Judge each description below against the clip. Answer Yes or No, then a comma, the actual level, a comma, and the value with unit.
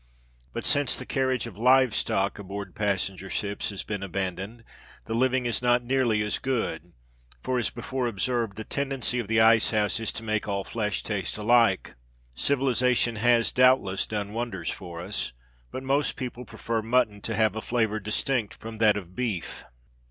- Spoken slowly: No, average, 175 wpm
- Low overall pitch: Yes, low, 110 Hz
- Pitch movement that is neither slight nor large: Yes, average, 3.4 semitones